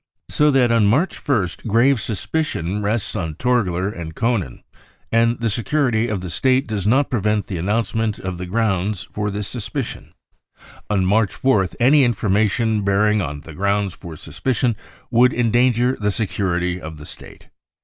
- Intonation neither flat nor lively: Yes, average, 4.1 semitones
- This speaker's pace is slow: No, average, 160 wpm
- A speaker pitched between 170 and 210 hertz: No, low, 105 Hz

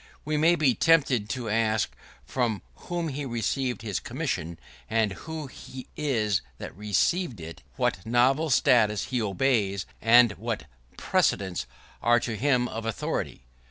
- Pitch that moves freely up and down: No, average, 4.3 semitones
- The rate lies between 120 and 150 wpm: Yes, average, 140 wpm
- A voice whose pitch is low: Yes, low, 120 Hz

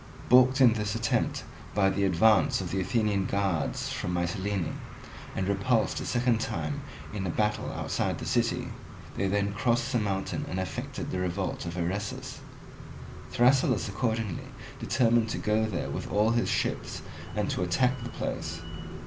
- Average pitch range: Yes, average, 3.6 semitones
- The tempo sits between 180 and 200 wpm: No, average, 155 wpm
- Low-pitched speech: Yes, low, 105 Hz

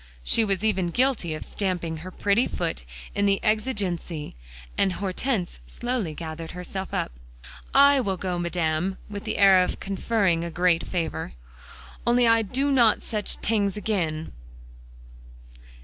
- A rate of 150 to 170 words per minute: No, average, 140 wpm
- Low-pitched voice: No, high, 190 Hz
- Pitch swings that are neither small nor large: Yes, average, 4.1 semitones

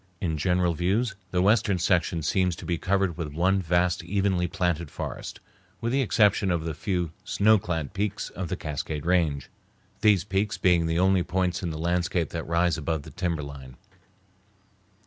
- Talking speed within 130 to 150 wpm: No, average, 170 wpm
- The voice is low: Yes, very low, 90 Hz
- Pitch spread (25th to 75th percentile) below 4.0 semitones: Yes, narrow, 2.6 semitones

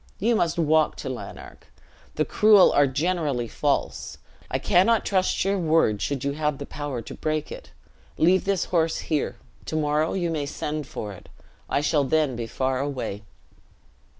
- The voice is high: No, medium, 155 Hz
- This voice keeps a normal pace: Yes, average, 170 wpm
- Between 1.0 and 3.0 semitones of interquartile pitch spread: No, average, 3.6 semitones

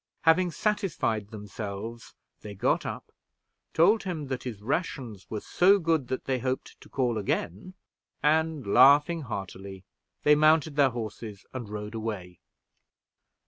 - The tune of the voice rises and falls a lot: Yes, wide, 6.9 semitones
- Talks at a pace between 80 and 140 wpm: Yes, slow, 135 wpm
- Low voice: Yes, low, 125 Hz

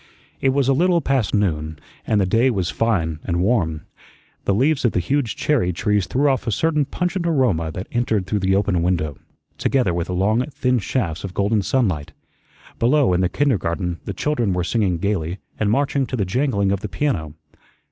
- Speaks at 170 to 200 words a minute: Yes, average, 190 wpm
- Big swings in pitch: Yes, wide, 6.6 semitones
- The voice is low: Yes, low, 105 Hz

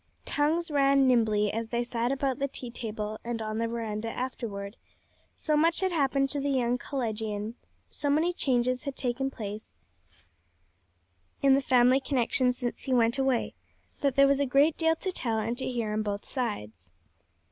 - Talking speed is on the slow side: No, average, 175 wpm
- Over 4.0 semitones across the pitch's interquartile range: No, average, 3.4 semitones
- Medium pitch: No, very high, 250 Hz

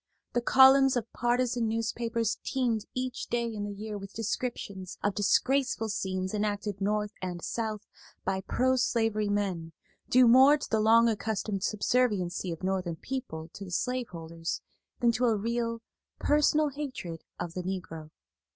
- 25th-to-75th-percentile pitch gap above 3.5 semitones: Yes, average, 4.1 semitones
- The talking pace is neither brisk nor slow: Yes, average, 150 wpm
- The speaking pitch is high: Yes, high, 220 Hz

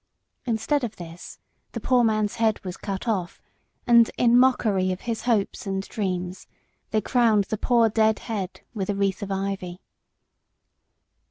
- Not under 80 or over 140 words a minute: No, average, 155 wpm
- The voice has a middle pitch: No, high, 210 Hz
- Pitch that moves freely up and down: No, average, 3.3 semitones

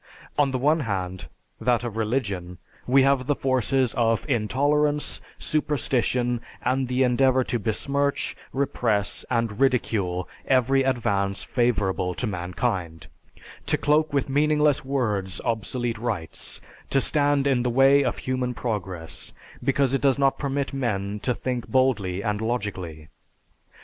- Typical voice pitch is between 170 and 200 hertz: No, low, 125 Hz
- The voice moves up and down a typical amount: Yes, average, 4.7 semitones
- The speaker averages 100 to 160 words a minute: Yes, slow, 135 wpm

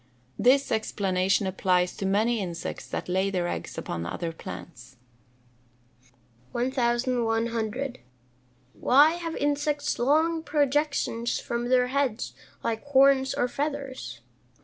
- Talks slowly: Yes, slow, 105 wpm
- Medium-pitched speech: No, high, 240 Hz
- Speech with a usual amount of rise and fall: No, wide, 6.3 semitones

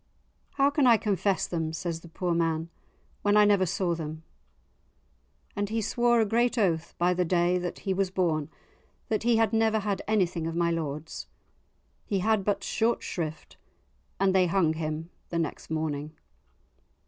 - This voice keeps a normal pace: Yes, average, 170 wpm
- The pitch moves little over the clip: No, average, 4.3 semitones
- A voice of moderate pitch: Yes, medium, 180 Hz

